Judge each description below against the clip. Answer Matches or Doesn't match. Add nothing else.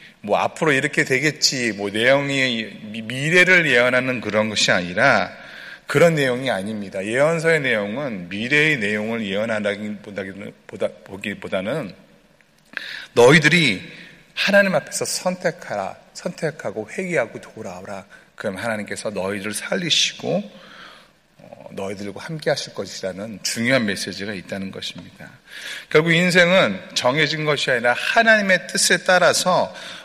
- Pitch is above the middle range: Doesn't match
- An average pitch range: Doesn't match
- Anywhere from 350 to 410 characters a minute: Doesn't match